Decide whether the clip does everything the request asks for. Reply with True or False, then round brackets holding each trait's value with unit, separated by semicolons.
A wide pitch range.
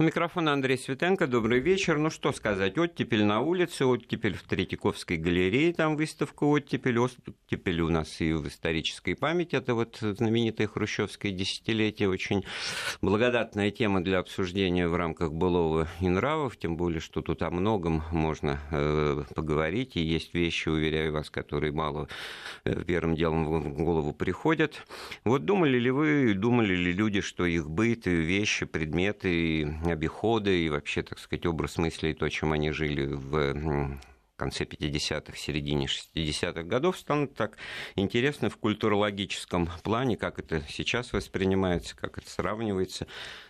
True (6.2 semitones)